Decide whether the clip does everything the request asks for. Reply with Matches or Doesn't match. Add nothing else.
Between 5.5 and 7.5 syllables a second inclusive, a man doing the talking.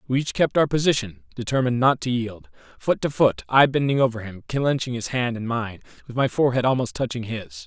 Matches